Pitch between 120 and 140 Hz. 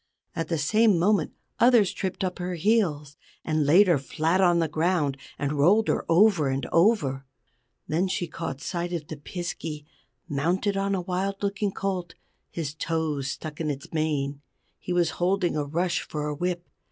No: medium, 170 Hz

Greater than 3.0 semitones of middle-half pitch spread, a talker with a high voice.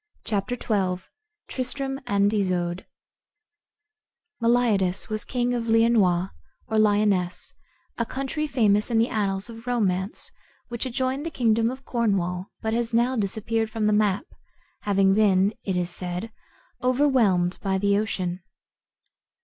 Yes: average, 3.8 semitones; high, 215 Hz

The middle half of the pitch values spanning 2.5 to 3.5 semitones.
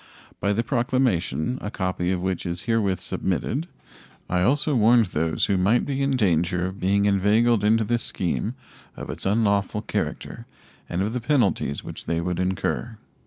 No: average, 4.4 semitones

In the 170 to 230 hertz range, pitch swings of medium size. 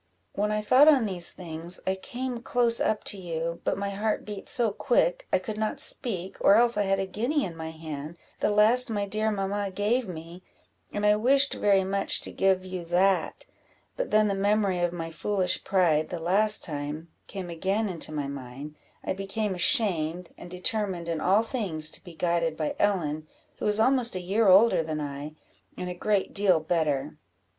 Yes: high, 190 Hz; average, 4.2 semitones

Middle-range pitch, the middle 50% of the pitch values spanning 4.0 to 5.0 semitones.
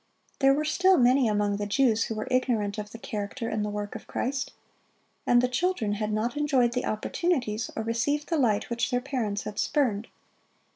No: high, 235 Hz; average, 4.3 semitones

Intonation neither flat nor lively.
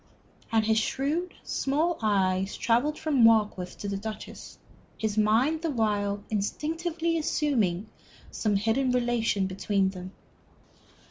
No: wide, 5.9 semitones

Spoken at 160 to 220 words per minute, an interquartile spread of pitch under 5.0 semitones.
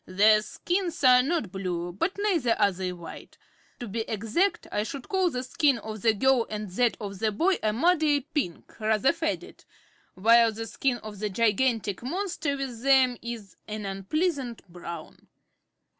No: average, 165 wpm; wide, 5.4 semitones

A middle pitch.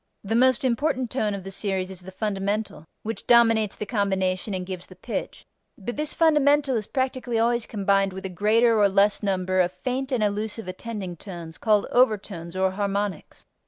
No: high, 205 Hz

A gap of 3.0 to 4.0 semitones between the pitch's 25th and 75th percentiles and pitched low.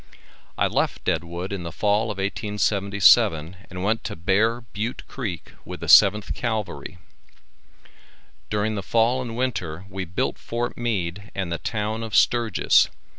Yes: average, 3.4 semitones; low, 105 Hz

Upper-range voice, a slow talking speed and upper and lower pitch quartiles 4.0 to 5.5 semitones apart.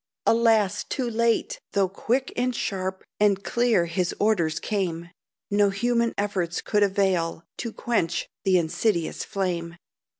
Yes: high, 200 Hz; slow, 130 wpm; average, 4.5 semitones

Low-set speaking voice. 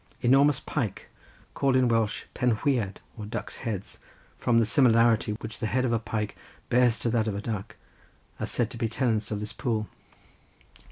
Yes: low, 115 Hz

